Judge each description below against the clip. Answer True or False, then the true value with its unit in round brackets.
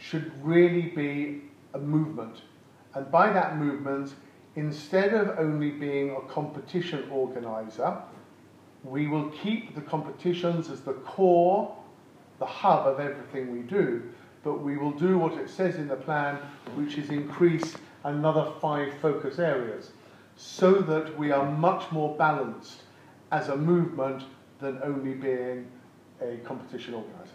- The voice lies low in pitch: False (150 Hz)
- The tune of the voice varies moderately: True (3.0 semitones)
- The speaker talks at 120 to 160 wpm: True (140 wpm)